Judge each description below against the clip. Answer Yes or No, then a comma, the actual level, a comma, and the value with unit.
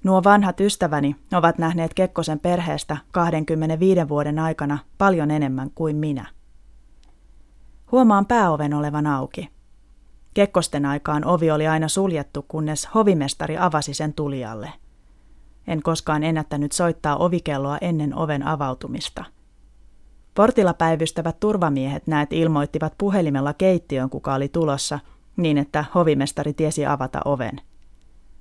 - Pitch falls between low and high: Yes, medium, 150 Hz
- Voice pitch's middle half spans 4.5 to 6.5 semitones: No, average, 3.3 semitones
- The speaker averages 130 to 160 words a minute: No, average, 110 wpm